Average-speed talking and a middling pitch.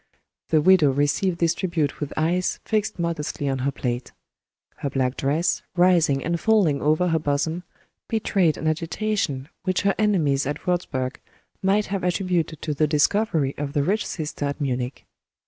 Yes: average, 160 wpm; medium, 160 Hz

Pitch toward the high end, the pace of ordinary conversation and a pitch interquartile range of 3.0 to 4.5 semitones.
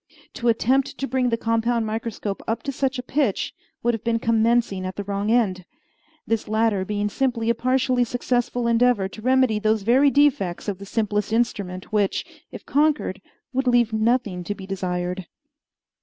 Yes: high, 230 Hz; average, 170 wpm; average, 3.4 semitones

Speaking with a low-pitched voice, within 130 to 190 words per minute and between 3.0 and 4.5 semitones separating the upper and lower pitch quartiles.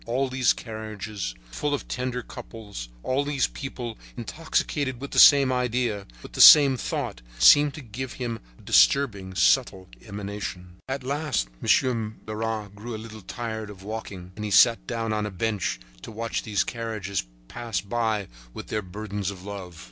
Yes: low, 110 Hz; average, 165 wpm; average, 3.8 semitones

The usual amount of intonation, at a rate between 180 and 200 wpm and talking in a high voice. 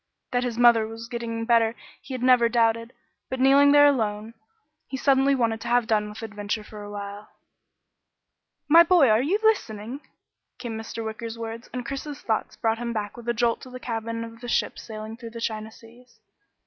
No: narrow, 2.2 semitones; average, 190 wpm; high, 230 Hz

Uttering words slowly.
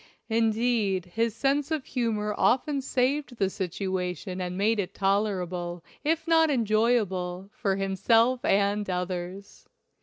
Yes: slow, 120 wpm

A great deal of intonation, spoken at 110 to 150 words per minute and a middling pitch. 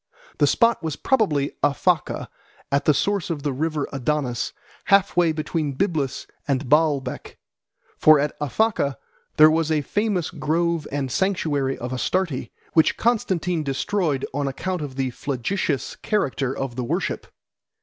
No: average, 4.3 semitones; average, 140 wpm; medium, 150 Hz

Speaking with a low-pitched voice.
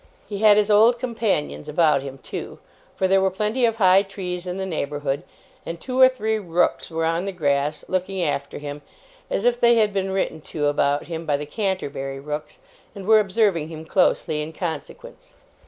No: medium, 180 Hz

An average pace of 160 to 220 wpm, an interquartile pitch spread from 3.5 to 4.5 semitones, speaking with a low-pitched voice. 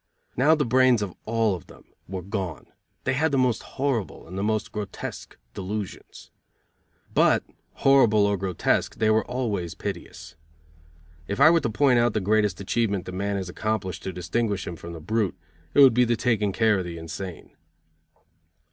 Yes: average, 175 wpm; average, 4.1 semitones; low, 105 Hz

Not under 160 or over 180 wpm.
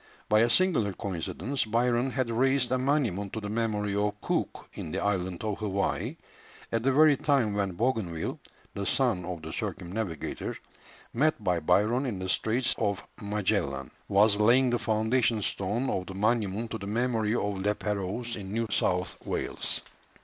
Yes: average, 165 wpm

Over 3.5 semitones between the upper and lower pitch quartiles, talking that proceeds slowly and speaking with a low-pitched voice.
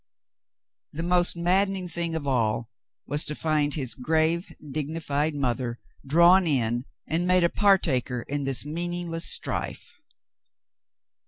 No: average, 4.1 semitones; slow, 130 wpm; medium, 155 Hz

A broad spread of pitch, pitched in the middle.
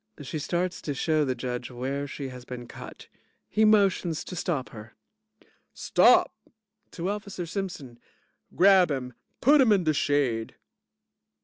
Yes: wide, 6.4 semitones; medium, 150 Hz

